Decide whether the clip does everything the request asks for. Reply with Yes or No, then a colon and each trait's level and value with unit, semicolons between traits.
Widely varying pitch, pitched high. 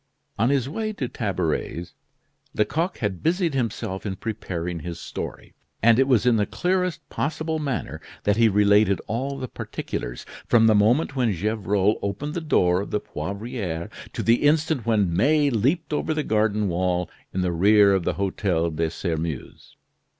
No: wide, 6.6 semitones; low, 105 Hz